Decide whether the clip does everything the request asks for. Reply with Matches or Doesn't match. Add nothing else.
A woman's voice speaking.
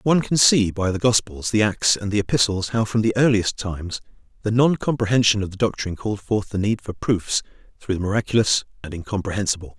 Doesn't match